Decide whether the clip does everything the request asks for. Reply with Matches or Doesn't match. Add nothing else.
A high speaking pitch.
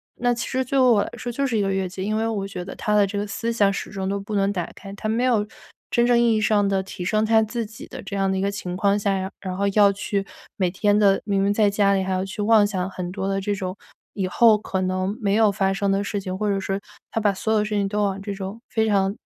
Matches